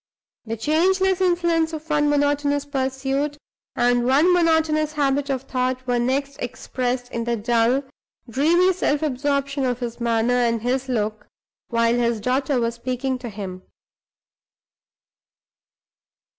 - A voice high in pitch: Yes, very high, 265 Hz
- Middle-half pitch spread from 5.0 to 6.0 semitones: No, average, 3.5 semitones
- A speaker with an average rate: No, slow, 130 wpm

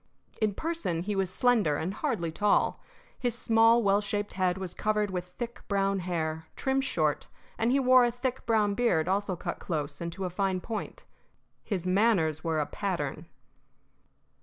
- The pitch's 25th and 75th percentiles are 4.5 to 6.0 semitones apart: Yes, average, 4.9 semitones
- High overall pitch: Yes, high, 195 Hz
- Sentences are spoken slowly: No, average, 170 wpm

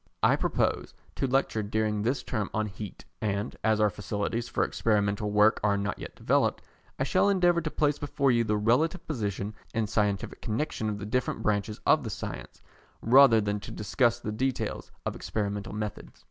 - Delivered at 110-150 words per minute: No, average, 185 wpm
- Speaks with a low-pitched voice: Yes, low, 110 Hz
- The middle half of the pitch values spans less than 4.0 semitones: Yes, average, 3.4 semitones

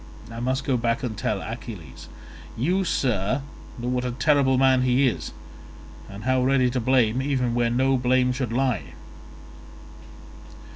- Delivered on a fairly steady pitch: Yes, narrow, 2.1 semitones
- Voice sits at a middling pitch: No, low, 125 Hz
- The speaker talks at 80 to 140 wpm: No, average, 150 wpm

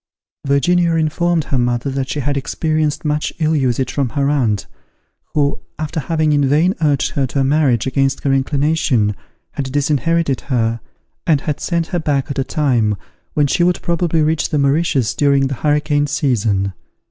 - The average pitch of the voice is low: No, medium, 145 Hz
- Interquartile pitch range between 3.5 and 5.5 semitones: No, average, 2.7 semitones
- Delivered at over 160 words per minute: Yes, average, 170 wpm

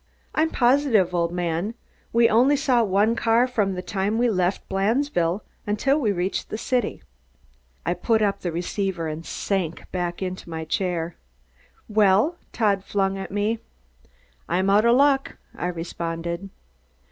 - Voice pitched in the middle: No, high, 195 Hz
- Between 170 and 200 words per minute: No, average, 145 wpm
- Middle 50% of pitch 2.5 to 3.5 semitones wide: No, average, 4.5 semitones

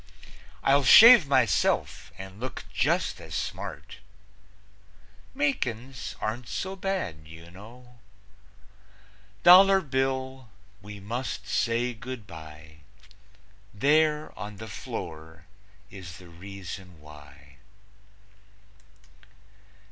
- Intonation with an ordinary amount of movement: No, wide, 7.6 semitones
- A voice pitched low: Yes, low, 110 Hz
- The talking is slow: Yes, slow, 85 wpm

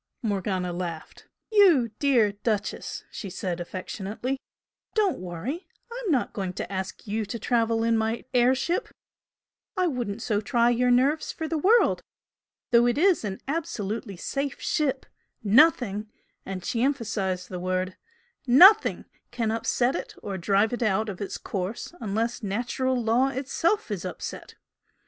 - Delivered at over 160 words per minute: No, average, 145 wpm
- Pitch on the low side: No, high, 230 Hz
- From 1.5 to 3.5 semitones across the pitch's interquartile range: No, average, 5.2 semitones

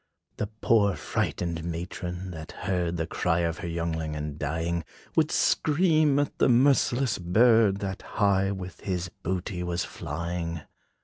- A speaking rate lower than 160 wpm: Yes, average, 140 wpm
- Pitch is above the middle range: No, very low, 90 Hz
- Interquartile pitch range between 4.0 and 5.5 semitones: No, average, 3.5 semitones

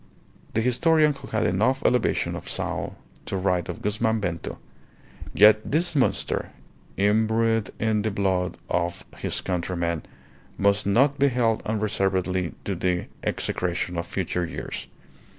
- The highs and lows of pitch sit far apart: No, average, 3.8 semitones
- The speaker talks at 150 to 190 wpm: No, slow, 135 wpm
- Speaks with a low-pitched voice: Yes, low, 100 Hz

